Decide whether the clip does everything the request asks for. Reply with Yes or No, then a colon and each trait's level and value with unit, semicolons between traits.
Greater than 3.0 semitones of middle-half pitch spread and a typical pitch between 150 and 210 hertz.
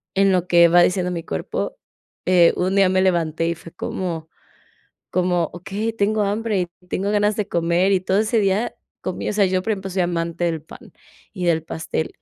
No: narrow, 2.6 semitones; medium, 185 Hz